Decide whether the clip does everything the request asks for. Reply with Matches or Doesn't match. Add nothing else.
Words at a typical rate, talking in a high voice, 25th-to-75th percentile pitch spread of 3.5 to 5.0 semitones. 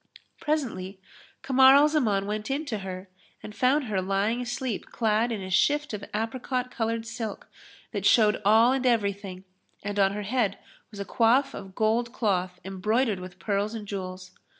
Matches